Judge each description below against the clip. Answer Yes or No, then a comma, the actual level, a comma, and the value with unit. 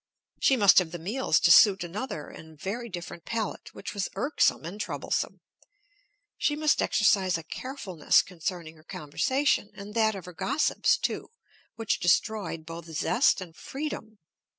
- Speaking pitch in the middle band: No, high, 195 Hz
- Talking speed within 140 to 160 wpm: Yes, average, 150 wpm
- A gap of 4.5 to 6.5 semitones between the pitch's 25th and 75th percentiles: Yes, average, 5.3 semitones